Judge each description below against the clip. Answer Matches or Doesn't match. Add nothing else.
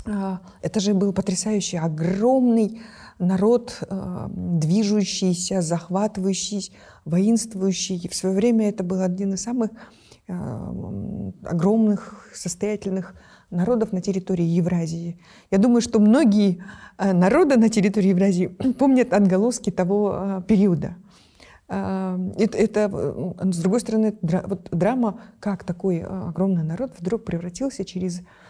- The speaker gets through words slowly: Matches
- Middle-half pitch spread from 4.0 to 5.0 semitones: Doesn't match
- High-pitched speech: Matches